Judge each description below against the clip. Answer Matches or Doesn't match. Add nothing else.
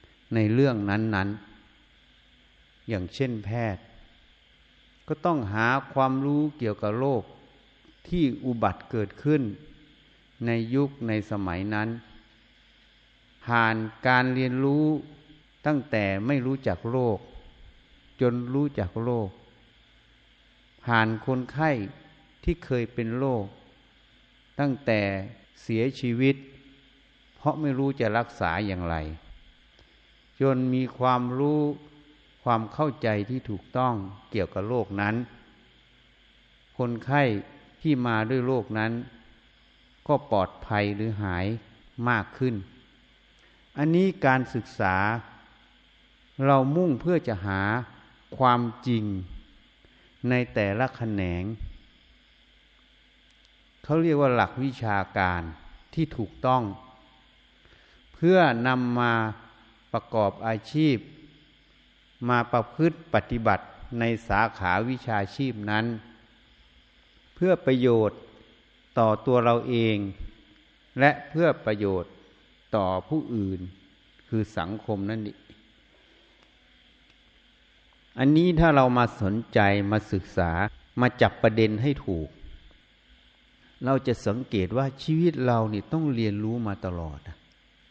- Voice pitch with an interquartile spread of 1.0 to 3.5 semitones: Doesn't match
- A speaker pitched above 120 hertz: Doesn't match